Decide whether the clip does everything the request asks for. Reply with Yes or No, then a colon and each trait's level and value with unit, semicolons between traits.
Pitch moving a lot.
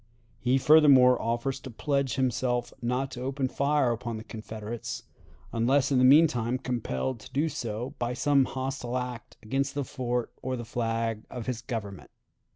No: narrow, 2.4 semitones